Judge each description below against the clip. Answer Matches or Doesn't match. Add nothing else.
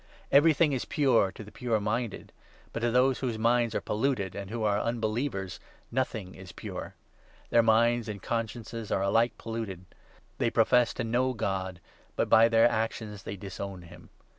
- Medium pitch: Doesn't match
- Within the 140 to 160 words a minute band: Doesn't match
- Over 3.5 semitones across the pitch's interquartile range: Doesn't match